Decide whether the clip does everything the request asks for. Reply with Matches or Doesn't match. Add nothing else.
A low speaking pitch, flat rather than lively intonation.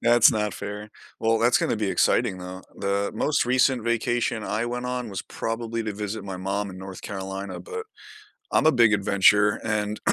Doesn't match